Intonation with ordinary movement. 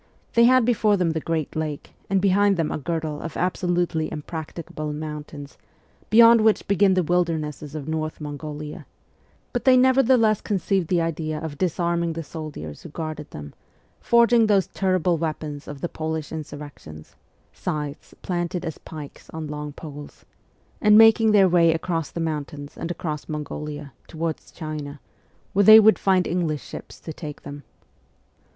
Yes: average, 3.6 semitones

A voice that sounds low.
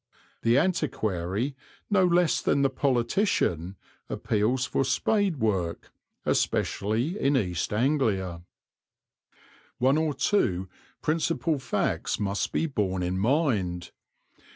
Yes: low, 125 Hz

